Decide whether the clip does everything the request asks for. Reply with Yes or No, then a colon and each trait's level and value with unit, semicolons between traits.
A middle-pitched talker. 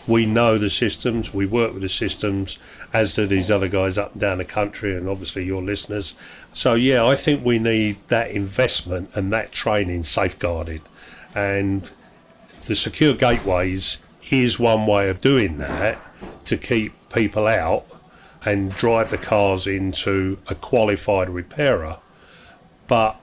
No: low, 100 Hz